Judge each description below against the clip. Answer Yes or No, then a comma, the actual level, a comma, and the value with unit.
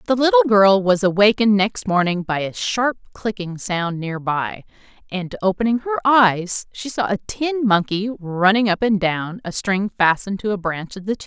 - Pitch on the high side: Yes, high, 205 Hz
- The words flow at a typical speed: Yes, average, 190 wpm